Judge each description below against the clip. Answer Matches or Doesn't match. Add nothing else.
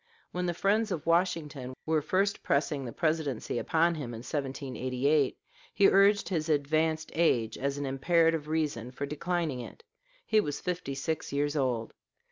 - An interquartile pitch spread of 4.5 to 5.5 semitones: Doesn't match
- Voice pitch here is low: Doesn't match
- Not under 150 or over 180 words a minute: Matches